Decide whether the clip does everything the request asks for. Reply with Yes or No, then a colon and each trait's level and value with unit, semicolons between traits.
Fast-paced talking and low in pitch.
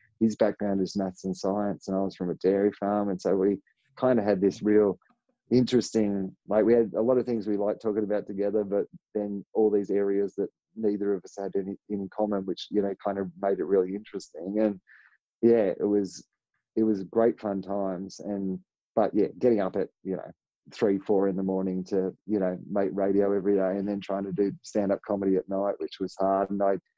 Yes: fast, 220 wpm; low, 100 Hz